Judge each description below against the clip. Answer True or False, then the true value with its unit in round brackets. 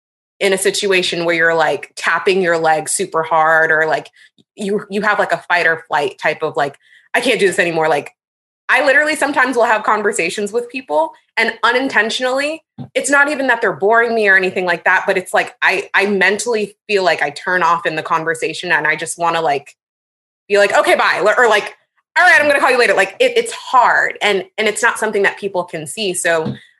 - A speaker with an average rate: False (220 wpm)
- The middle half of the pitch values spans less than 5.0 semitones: False (5.6 semitones)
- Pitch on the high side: True (200 Hz)